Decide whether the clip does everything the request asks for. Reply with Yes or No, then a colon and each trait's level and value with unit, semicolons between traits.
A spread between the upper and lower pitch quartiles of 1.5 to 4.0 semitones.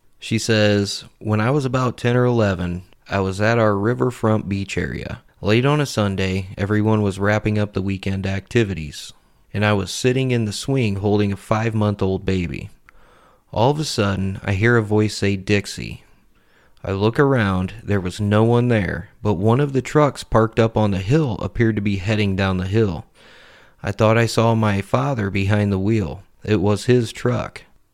Yes: average, 2.9 semitones